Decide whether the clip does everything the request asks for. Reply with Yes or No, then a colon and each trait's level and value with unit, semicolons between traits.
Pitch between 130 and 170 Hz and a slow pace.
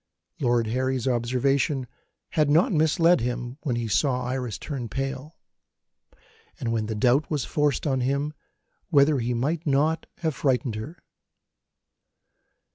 Yes: low, 135 Hz; slow, 130 wpm